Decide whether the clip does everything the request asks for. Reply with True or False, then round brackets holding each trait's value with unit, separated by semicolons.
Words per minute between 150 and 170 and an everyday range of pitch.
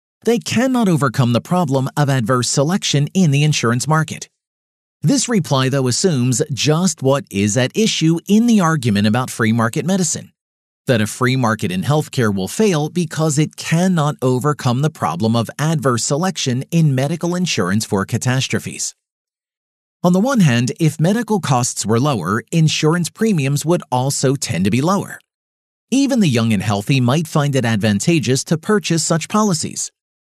False (160 wpm; 6.0 semitones)